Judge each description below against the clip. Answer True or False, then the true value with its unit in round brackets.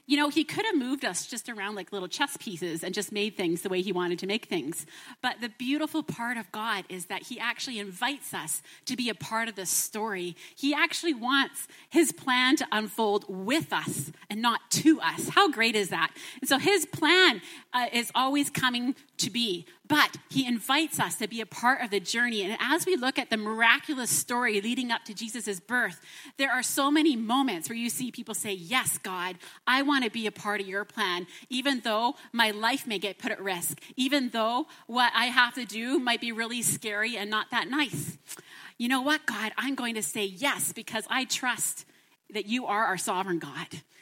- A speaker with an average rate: False (215 wpm)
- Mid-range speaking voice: False (235 Hz)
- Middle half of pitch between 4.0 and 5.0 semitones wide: True (4.7 semitones)